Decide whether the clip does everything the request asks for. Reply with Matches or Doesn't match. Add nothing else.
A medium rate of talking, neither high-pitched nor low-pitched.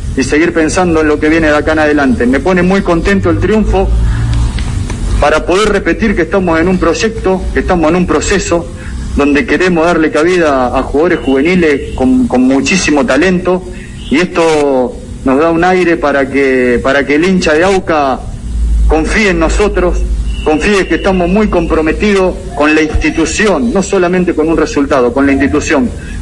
Matches